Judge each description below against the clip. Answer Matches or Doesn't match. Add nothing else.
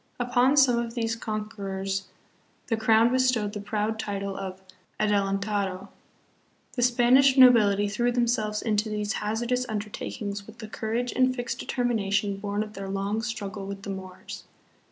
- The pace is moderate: Matches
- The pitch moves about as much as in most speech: Matches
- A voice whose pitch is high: Matches